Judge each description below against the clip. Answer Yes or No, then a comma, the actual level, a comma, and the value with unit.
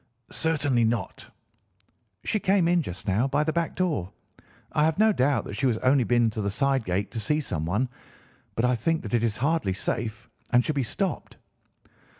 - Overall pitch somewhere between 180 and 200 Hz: No, low, 125 Hz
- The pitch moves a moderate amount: No, wide, 5.9 semitones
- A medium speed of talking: Yes, average, 190 wpm